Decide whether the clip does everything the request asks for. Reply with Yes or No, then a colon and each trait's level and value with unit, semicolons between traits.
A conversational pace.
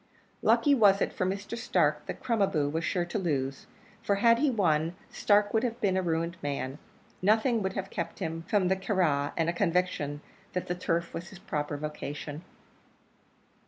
Yes: average, 190 wpm